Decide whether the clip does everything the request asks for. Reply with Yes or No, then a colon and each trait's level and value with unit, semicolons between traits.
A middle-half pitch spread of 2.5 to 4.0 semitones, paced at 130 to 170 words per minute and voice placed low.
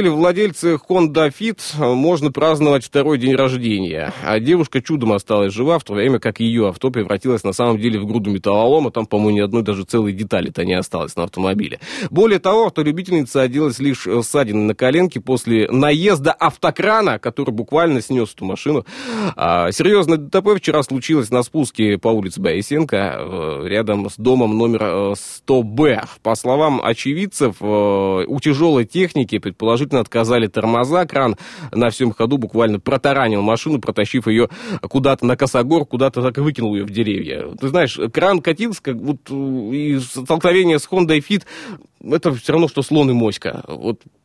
No: wide, 5.6 semitones; average, 155 wpm; low, 130 Hz